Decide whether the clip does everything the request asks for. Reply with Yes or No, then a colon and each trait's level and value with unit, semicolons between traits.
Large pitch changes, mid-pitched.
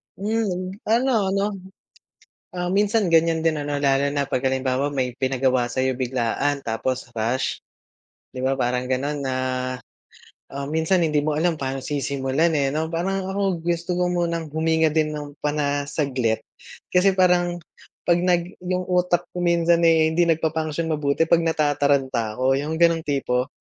No: average, 4.3 semitones; medium, 155 Hz